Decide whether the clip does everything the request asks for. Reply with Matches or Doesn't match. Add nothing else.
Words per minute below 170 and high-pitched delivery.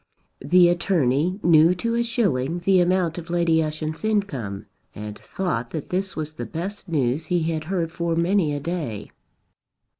Doesn't match